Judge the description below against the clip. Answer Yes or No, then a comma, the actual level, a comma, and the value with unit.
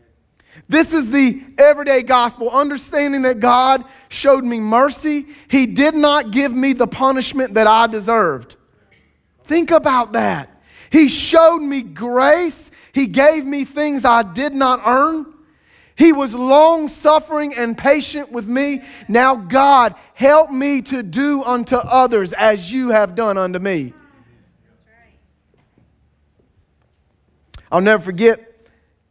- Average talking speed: No, slow, 125 wpm